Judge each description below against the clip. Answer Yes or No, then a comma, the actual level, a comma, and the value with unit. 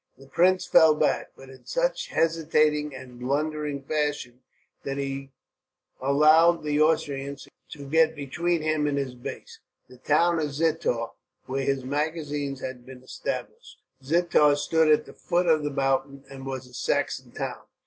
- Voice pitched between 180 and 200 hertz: No, medium, 145 Hz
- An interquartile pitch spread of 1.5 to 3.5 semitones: Yes, average, 2.7 semitones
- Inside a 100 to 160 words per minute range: Yes, average, 155 wpm